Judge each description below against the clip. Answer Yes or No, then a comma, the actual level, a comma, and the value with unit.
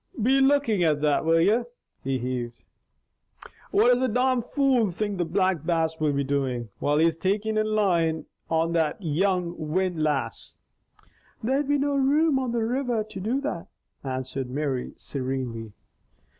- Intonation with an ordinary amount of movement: No, wide, 8.0 semitones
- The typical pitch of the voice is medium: Yes, medium, 175 Hz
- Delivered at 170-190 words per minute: No, average, 155 wpm